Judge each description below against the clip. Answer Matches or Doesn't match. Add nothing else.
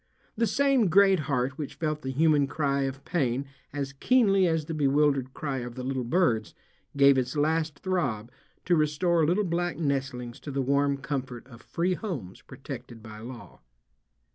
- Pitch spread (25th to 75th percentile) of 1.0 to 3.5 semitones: Doesn't match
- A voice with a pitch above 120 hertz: Matches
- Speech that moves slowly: Doesn't match